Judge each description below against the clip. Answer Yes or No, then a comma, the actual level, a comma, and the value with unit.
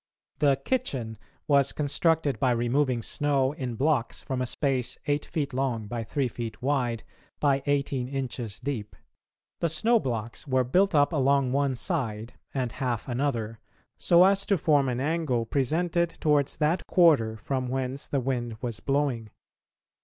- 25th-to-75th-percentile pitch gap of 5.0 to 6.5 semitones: No, average, 3.3 semitones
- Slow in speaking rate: No, average, 155 wpm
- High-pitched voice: No, low, 135 Hz